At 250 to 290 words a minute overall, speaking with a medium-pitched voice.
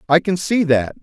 No: fast, 235 wpm; medium, 165 Hz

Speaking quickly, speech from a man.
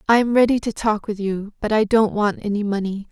No: fast, 250 wpm; female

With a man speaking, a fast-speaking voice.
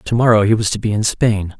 Yes: male; fast, 300 wpm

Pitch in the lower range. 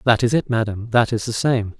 Yes: low, 115 Hz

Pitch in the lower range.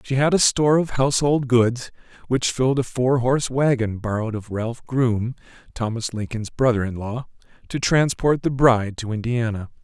Yes: low, 125 Hz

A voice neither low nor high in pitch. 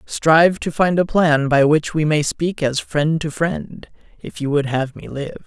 Yes: medium, 155 Hz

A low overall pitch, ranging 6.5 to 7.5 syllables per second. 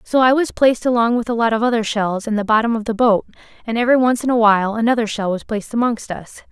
No: high, 230 Hz; 6.7 syllables/s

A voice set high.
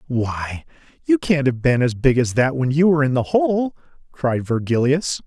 No: medium, 140 Hz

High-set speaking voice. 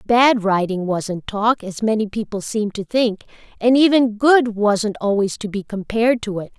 Yes: high, 215 Hz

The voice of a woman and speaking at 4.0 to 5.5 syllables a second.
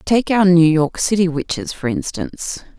Yes: female; 4.7 syllables/s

